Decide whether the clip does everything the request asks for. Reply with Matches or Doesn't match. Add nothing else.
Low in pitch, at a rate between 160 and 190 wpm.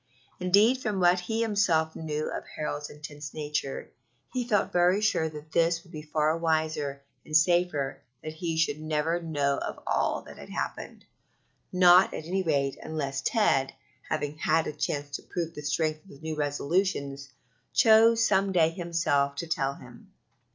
Doesn't match